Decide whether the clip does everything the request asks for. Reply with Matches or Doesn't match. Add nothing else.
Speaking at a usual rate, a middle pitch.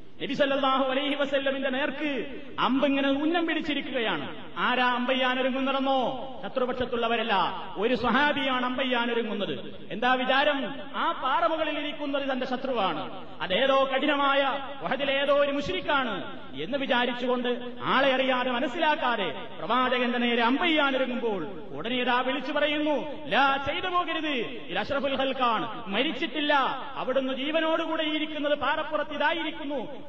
Doesn't match